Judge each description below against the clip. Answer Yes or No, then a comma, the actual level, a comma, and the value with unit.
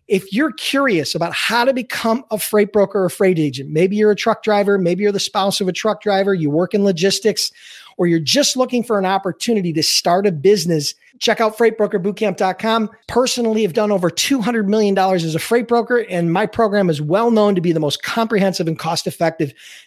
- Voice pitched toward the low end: No, high, 205 Hz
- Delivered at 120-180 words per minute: No, fast, 205 wpm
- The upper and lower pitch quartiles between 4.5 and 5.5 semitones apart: No, average, 3.7 semitones